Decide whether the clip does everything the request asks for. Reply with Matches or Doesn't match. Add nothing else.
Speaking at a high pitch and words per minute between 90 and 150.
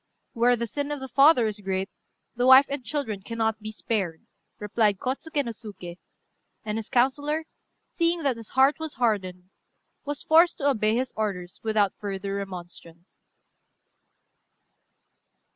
Matches